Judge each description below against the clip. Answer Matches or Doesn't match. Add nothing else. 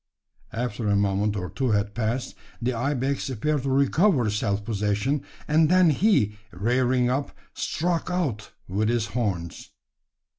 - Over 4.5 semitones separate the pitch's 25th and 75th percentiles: Matches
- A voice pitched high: Doesn't match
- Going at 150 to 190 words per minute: Doesn't match